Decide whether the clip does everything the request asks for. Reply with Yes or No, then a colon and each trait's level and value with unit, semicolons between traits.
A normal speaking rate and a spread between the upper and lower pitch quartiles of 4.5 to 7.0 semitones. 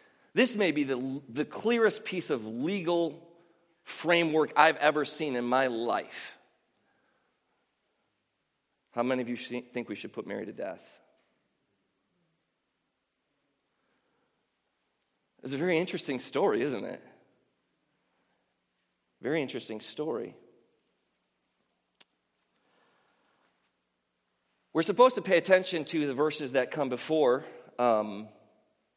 No: slow, 100 wpm; average, 5.2 semitones